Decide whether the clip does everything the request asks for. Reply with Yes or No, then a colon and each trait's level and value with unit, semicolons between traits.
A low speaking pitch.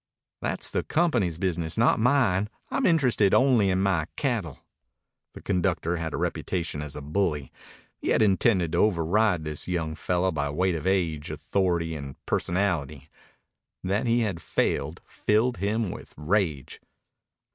Yes: very low, 90 Hz